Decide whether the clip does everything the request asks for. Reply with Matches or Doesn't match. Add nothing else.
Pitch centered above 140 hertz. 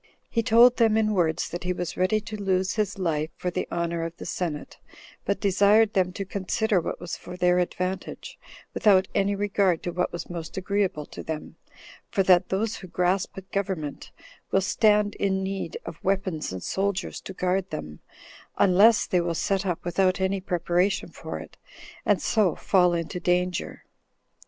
Matches